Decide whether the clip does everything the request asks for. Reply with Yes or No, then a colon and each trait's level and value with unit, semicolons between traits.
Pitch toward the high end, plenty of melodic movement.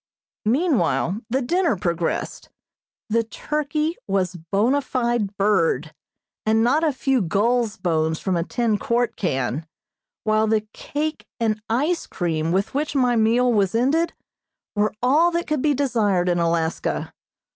Yes: high, 225 Hz; wide, 6.5 semitones